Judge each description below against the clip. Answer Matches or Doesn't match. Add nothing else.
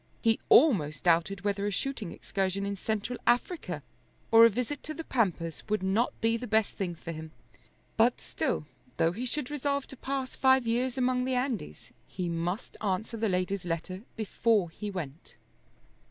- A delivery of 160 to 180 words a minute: Matches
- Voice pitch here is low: Doesn't match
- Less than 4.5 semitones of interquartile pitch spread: Doesn't match